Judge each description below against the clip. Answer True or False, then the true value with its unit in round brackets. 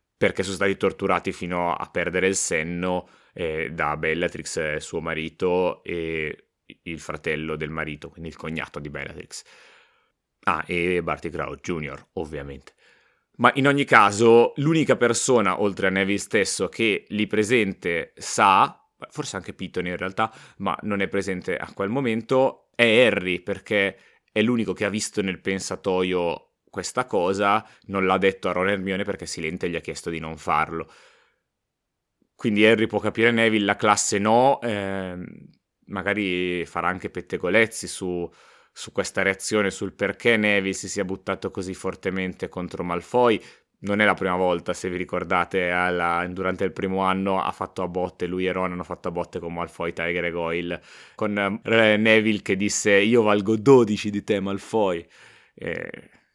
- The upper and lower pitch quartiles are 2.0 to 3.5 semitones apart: True (2.9 semitones)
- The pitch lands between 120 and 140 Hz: False (95 Hz)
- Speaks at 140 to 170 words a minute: True (160 wpm)